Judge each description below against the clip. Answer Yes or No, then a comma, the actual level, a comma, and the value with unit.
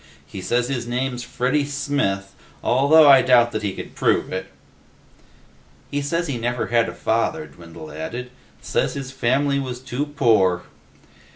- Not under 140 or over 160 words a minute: Yes, average, 155 wpm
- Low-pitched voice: Yes, low, 125 Hz